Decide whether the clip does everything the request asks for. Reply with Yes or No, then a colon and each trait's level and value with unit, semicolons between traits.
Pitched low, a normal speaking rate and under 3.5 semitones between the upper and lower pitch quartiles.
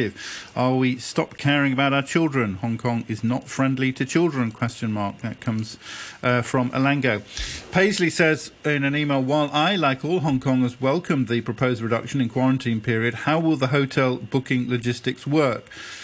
Yes: low, 130 Hz; average, 170 wpm; average, 3.1 semitones